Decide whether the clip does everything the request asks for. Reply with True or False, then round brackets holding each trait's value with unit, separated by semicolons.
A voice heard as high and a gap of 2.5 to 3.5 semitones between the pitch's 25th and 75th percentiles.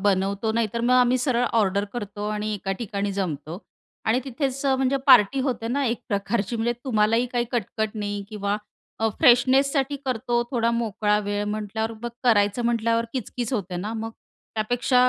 True (225 Hz; 3.0 semitones)